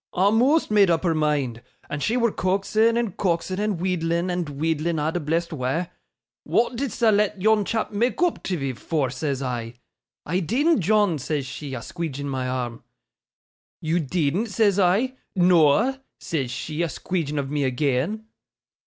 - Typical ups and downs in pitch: No, wide, 6.3 semitones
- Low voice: No, medium, 170 Hz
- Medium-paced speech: Yes, average, 165 wpm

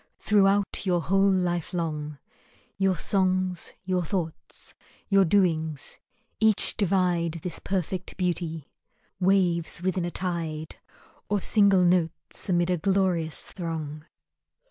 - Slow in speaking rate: Yes, slow, 110 wpm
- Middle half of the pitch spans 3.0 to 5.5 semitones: No, narrow, 2.6 semitones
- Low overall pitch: No, medium, 180 Hz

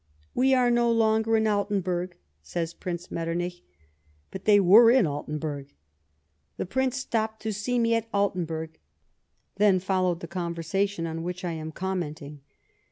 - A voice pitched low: No, medium, 185 Hz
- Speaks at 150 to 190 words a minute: Yes, average, 165 wpm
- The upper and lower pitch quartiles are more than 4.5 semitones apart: Yes, average, 4.9 semitones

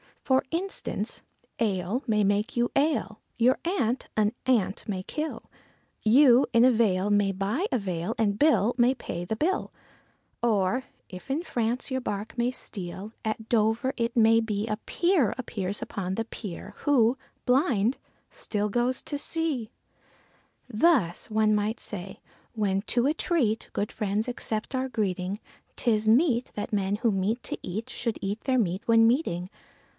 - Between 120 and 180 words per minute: Yes, average, 160 wpm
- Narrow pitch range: No, average, 3.8 semitones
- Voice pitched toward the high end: Yes, high, 225 Hz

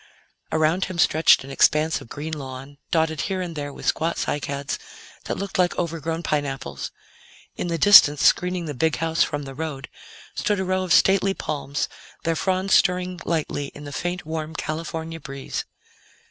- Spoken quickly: No, average, 170 wpm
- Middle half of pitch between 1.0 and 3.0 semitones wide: No, average, 3.5 semitones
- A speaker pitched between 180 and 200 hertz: No, medium, 160 Hz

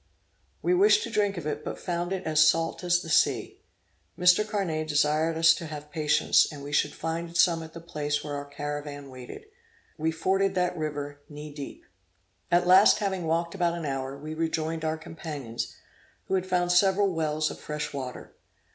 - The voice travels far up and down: No, average, 3.0 semitones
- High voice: No, medium, 160 Hz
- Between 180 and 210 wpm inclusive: Yes, average, 185 wpm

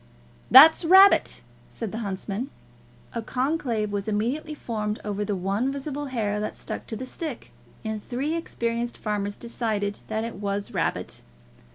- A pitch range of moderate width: Yes, average, 4.3 semitones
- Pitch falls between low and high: No, high, 225 Hz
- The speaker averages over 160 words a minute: No, average, 150 wpm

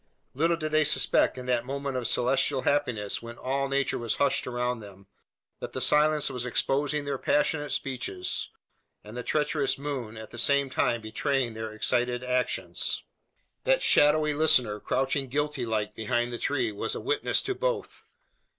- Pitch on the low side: Yes, low, 130 Hz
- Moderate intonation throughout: Yes, average, 3.6 semitones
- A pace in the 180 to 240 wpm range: No, average, 165 wpm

